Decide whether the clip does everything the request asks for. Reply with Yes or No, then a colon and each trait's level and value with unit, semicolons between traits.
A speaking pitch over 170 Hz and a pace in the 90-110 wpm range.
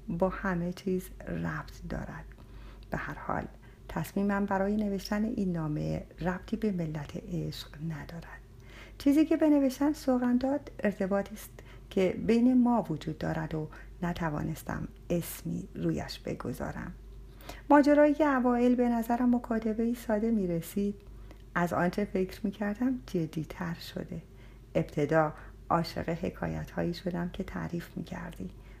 No: medium, 185 Hz; average, 130 wpm